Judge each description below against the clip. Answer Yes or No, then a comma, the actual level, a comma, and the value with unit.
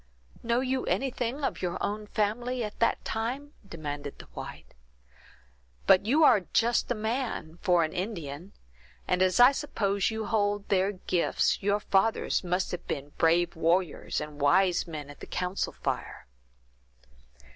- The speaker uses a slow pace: No, average, 150 wpm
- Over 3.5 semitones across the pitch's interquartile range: Yes, average, 4.9 semitones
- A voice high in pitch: Yes, high, 200 Hz